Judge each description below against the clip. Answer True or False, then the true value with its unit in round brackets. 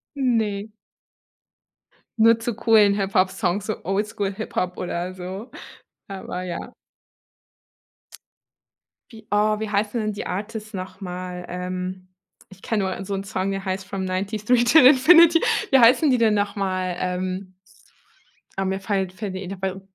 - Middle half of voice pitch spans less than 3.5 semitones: True (2.6 semitones)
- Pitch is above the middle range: True (195 Hz)